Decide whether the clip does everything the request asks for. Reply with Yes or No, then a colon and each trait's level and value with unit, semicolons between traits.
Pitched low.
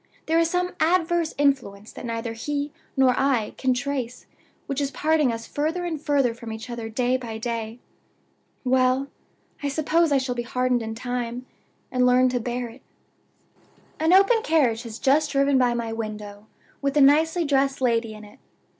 No: very high, 255 Hz